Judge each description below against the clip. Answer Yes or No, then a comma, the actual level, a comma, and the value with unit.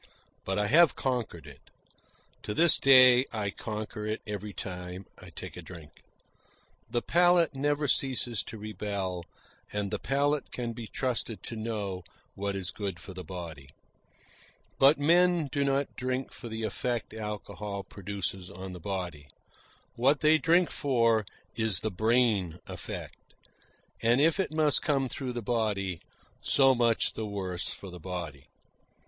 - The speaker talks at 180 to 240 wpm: No, average, 150 wpm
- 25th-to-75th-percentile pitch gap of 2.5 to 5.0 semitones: No, wide, 5.6 semitones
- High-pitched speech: No, low, 110 Hz